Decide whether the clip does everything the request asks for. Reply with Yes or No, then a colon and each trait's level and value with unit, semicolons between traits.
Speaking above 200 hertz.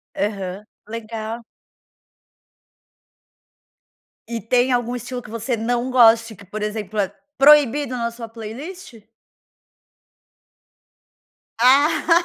Yes: high, 230 Hz